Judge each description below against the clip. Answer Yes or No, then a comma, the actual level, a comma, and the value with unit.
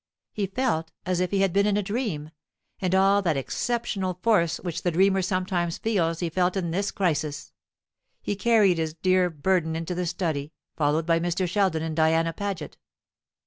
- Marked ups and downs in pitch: No, average, 3.2 semitones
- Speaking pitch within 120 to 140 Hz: No, medium, 180 Hz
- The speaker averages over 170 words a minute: Yes, average, 180 wpm